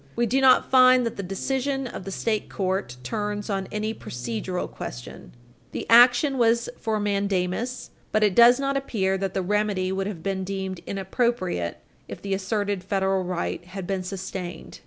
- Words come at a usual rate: Yes, average, 170 wpm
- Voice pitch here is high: Yes, high, 200 Hz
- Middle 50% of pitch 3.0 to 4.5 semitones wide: Yes, average, 3.8 semitones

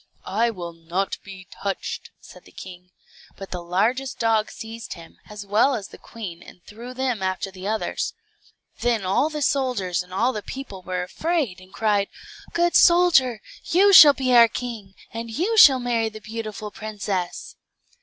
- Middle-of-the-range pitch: No, high, 220 Hz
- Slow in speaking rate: No, average, 165 wpm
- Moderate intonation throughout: Yes, average, 4.9 semitones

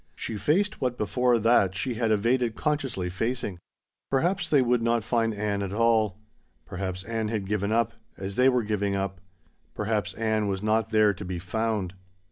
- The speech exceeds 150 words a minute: Yes, average, 175 wpm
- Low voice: Yes, low, 110 Hz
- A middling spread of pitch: Yes, average, 3.0 semitones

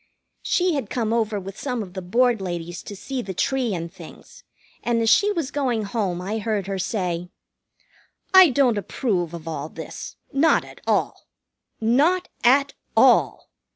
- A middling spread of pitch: No, wide, 5.9 semitones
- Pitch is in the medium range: No, high, 220 Hz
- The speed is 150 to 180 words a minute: Yes, average, 165 wpm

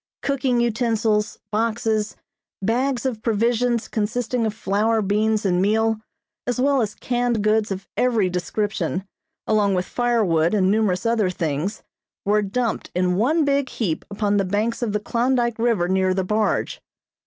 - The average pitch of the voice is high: Yes, high, 215 Hz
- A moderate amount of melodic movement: Yes, average, 3.0 semitones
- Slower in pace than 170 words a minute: Yes, average, 150 wpm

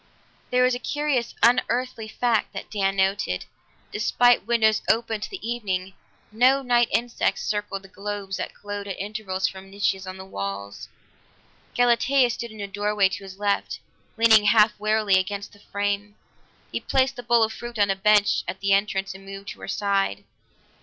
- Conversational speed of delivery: Yes, average, 175 wpm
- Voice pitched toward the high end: Yes, high, 205 Hz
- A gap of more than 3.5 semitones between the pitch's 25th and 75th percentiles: No, average, 3.2 semitones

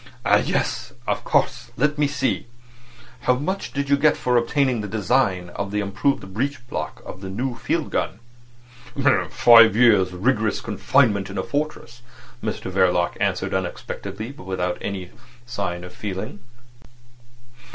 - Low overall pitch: Yes, low, 110 Hz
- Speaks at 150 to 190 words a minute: No, average, 140 wpm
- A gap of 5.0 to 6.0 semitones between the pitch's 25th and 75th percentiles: Yes, wide, 5.6 semitones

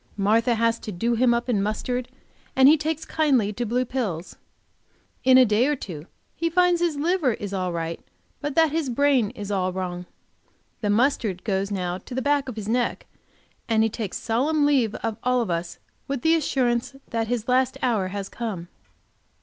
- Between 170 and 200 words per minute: Yes, average, 190 wpm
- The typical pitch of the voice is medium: No, high, 235 Hz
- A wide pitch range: No, average, 4.8 semitones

